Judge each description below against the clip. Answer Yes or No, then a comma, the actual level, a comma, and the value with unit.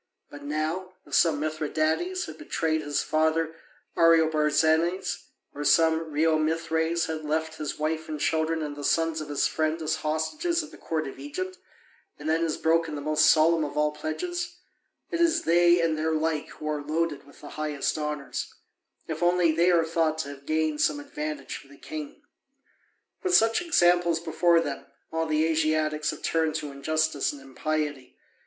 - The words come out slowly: No, average, 175 wpm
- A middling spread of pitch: No, narrow, 1.4 semitones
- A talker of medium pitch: Yes, medium, 155 Hz